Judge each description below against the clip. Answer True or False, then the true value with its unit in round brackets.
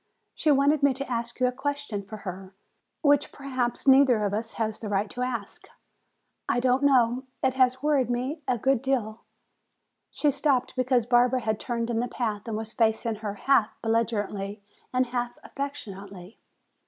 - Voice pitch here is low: False (245 Hz)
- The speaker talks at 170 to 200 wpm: True (175 wpm)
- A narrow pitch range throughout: False (3.4 semitones)